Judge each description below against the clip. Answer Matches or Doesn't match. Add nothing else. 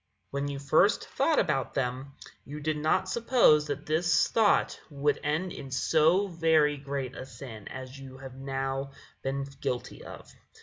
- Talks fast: Doesn't match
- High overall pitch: Doesn't match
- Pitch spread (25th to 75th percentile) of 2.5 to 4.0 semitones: Matches